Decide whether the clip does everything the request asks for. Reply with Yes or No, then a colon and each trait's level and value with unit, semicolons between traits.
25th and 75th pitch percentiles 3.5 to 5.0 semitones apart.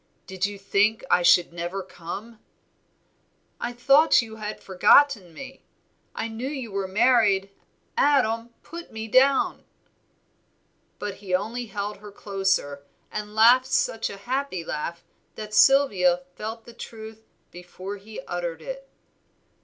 Yes: average, 4.1 semitones